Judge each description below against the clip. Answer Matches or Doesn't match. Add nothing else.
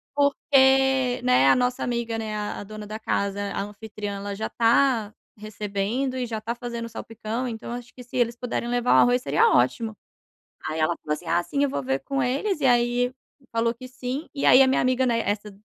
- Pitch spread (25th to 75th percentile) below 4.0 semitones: Matches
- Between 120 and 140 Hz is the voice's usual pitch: Doesn't match